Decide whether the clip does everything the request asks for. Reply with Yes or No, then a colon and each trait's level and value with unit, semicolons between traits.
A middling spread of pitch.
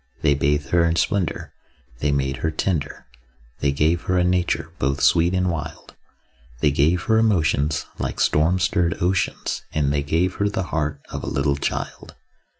Yes: average, 3.7 semitones